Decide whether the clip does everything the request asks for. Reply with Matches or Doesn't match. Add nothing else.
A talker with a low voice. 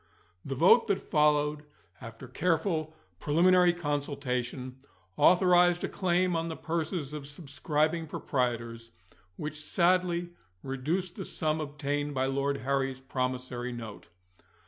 Doesn't match